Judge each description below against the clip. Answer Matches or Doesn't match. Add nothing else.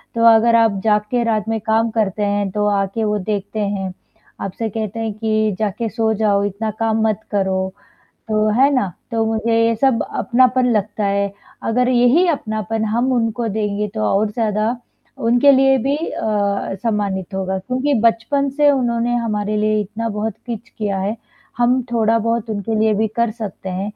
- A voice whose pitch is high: Matches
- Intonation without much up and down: Matches